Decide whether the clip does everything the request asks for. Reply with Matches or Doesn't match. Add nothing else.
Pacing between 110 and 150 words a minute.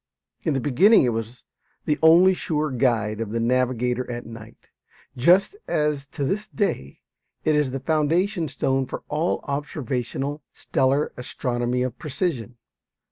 Matches